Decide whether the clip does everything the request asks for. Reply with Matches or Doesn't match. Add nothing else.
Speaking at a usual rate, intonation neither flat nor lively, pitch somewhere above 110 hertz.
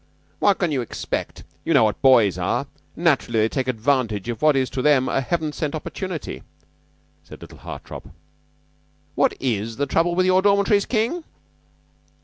Doesn't match